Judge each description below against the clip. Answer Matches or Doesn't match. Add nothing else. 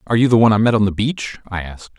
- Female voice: Doesn't match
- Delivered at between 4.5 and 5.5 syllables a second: Doesn't match